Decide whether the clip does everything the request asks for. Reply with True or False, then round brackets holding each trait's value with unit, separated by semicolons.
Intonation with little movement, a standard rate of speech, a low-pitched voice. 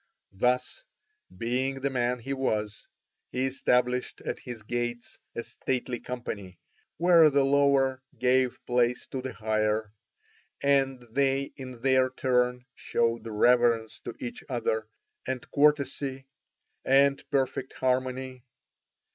False (2.0 semitones; 115 wpm; 125 Hz)